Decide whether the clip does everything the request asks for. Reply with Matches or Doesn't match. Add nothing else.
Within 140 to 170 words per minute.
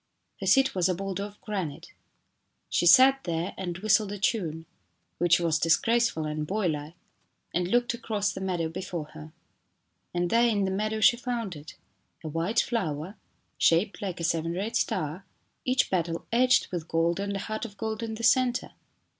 Doesn't match